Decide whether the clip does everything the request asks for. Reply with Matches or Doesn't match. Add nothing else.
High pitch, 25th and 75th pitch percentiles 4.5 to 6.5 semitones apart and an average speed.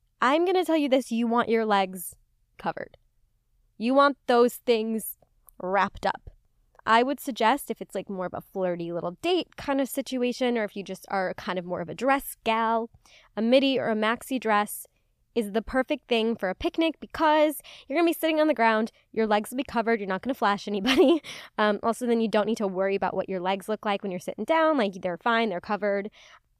Doesn't match